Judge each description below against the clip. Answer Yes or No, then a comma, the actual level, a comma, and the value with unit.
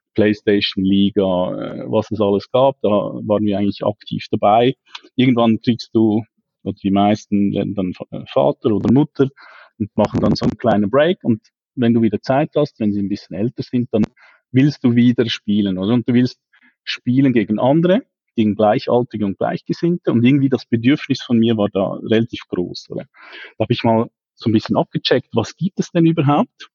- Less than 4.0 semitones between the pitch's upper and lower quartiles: No, average, 4.3 semitones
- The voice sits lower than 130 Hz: Yes, low, 115 Hz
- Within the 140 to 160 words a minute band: No, average, 180 wpm